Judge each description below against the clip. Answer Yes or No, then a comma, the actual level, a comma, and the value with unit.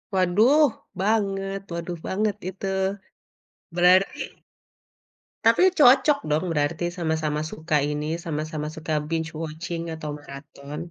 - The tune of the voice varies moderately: Yes, average, 4.1 semitones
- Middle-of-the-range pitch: Yes, medium, 165 Hz